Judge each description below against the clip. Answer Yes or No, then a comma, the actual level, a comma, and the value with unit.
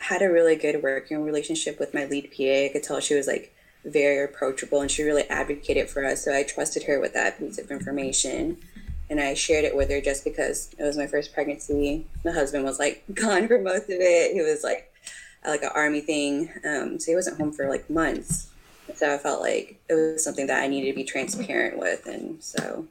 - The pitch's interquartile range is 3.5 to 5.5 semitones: No, narrow, 2.6 semitones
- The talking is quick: Yes, fast, 225 wpm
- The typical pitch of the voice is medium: Yes, medium, 145 Hz